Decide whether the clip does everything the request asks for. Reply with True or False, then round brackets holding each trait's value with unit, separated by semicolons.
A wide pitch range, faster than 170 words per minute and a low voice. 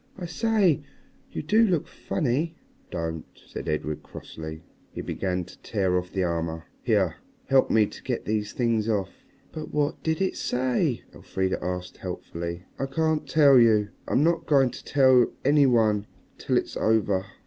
False (8.3 semitones; 160 wpm; 115 Hz)